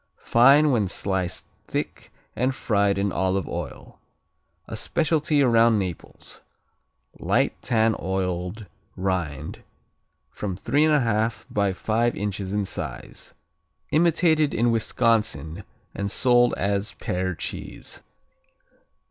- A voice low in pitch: Yes, low, 105 Hz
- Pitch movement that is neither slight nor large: Yes, average, 4.3 semitones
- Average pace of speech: No, slow, 105 wpm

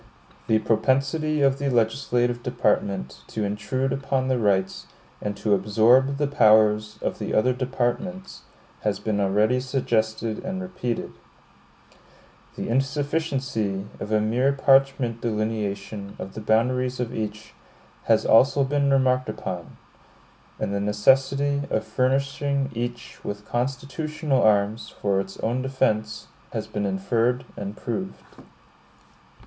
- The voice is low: Yes, low, 120 Hz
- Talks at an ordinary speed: No, slow, 125 wpm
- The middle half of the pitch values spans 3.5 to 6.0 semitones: Yes, average, 4.1 semitones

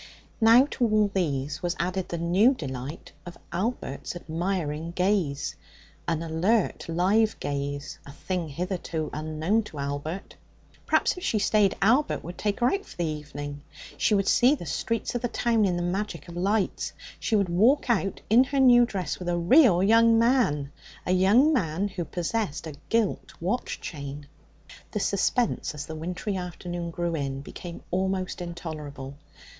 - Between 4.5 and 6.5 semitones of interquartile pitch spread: Yes, average, 5.3 semitones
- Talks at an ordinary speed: Yes, average, 165 wpm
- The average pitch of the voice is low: No, medium, 180 Hz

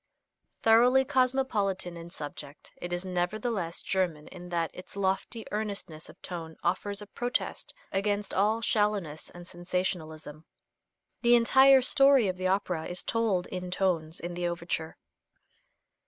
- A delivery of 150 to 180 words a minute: No, slow, 135 wpm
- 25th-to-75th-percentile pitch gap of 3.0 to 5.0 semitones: Yes, average, 3.9 semitones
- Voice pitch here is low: No, medium, 185 Hz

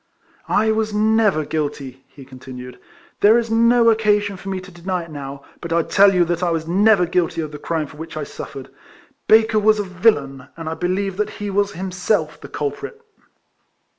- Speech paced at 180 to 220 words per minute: Yes, average, 195 wpm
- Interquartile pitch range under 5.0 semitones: No, average, 5.3 semitones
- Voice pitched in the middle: Yes, medium, 180 Hz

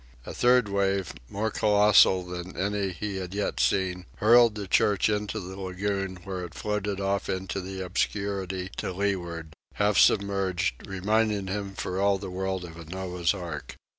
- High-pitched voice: No, very low, 95 Hz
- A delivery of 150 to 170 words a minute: Yes, average, 165 wpm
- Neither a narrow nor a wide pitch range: No, narrow, 1.9 semitones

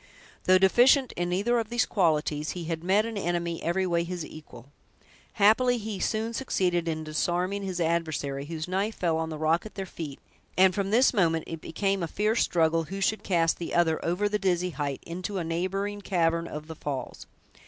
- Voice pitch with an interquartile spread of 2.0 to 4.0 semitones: Yes, average, 3.6 semitones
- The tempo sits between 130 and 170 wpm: No, average, 195 wpm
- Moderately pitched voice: Yes, medium, 175 Hz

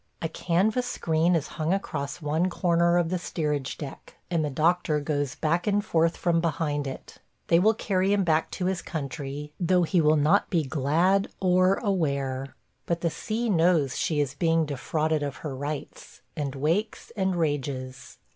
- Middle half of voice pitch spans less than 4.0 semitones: Yes, average, 3.6 semitones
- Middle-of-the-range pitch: Yes, medium, 165 Hz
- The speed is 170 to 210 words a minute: Yes, average, 175 wpm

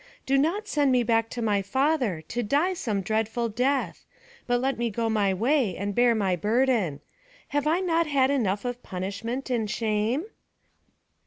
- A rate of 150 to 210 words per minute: Yes, average, 170 wpm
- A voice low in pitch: No, high, 235 Hz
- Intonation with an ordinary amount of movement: Yes, average, 4.6 semitones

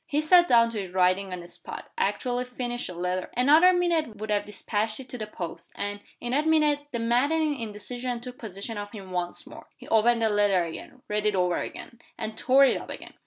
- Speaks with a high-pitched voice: Yes, high, 230 Hz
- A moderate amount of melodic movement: Yes, average, 4.2 semitones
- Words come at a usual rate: No, fast, 220 wpm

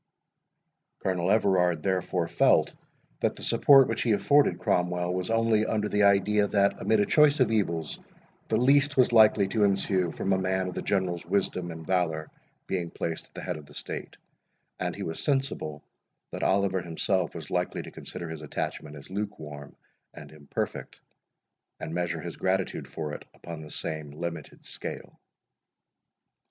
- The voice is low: Yes, very low, 95 Hz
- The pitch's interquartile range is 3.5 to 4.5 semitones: Yes, average, 4.0 semitones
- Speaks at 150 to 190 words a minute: Yes, average, 165 wpm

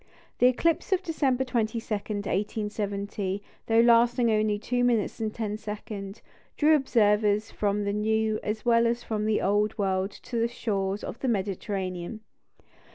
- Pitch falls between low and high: No, high, 215 Hz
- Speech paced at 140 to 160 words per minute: Yes, average, 150 wpm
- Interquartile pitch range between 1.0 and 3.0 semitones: Yes, narrow, 2.4 semitones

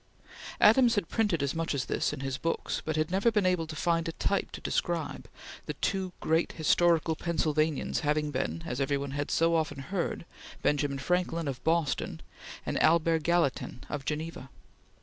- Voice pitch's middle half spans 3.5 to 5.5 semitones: No, average, 3.0 semitones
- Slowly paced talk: No, average, 175 wpm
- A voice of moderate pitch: Yes, medium, 160 Hz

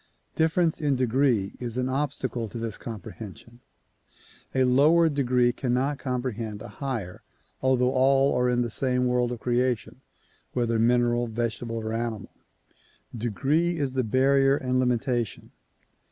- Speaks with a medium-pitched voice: No, low, 125 Hz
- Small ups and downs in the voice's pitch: Yes, narrow, 2.3 semitones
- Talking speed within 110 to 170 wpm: Yes, slow, 135 wpm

